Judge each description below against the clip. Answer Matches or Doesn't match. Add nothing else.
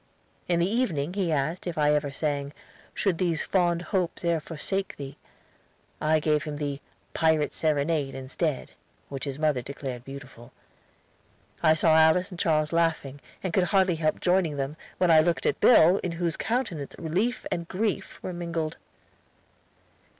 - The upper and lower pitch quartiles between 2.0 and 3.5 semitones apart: Matches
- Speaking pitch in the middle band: Matches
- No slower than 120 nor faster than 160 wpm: Matches